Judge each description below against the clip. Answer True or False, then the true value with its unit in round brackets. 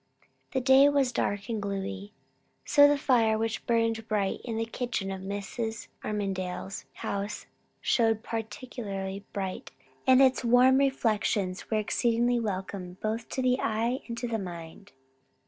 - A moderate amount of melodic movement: True (3.6 semitones)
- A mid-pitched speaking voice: False (220 Hz)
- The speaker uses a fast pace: False (145 wpm)